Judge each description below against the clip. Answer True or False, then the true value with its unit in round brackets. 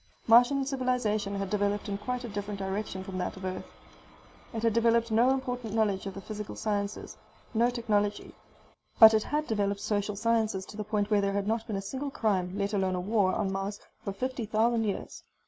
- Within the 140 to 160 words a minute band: False (200 wpm)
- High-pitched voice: True (210 Hz)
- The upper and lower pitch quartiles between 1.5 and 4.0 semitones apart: True (2.6 semitones)